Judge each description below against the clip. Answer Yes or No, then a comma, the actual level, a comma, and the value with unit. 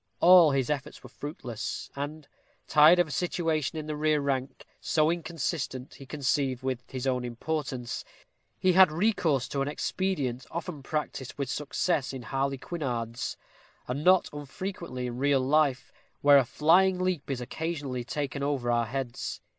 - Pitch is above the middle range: No, medium, 140 Hz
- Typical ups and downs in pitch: Yes, average, 3.4 semitones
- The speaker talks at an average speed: Yes, average, 155 wpm